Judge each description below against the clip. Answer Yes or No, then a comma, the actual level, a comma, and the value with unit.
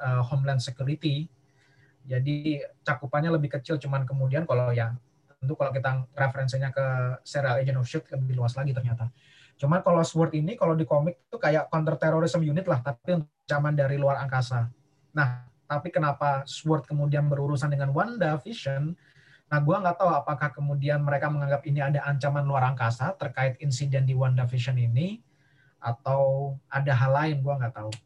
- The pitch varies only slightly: Yes, narrow, 1.9 semitones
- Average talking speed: No, fast, 165 wpm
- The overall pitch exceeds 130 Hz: Yes, medium, 140 Hz